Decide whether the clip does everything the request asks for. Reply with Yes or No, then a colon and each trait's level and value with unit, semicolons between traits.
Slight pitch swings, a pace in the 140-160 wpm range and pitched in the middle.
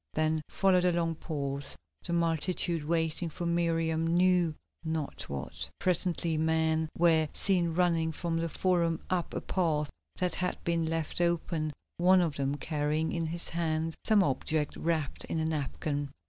Yes: narrow, 1.5 semitones; average, 155 wpm; medium, 165 Hz